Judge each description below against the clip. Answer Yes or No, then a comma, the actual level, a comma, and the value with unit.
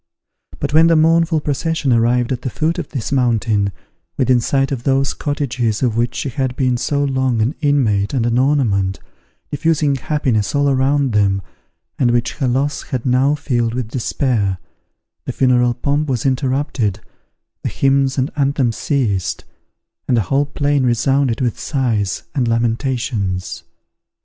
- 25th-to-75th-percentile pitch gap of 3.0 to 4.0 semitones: Yes, average, 3.3 semitones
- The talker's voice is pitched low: Yes, low, 130 Hz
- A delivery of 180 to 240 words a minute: No, average, 155 wpm